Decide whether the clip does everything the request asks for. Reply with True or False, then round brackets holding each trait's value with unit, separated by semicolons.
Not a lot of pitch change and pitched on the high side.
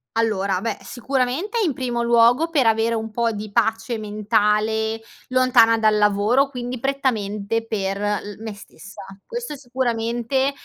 False (3.1 semitones; 225 Hz)